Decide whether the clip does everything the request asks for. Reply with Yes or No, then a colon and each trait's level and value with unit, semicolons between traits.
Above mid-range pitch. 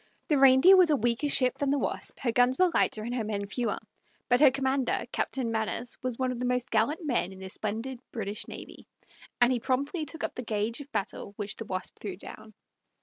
Yes: high, 245 Hz